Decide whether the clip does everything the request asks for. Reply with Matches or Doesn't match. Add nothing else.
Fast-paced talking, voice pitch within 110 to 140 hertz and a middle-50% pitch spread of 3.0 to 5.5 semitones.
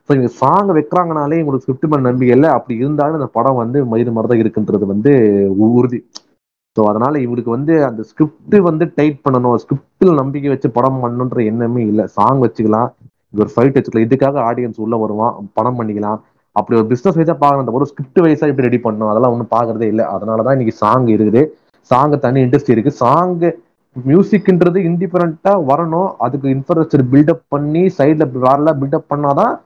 Matches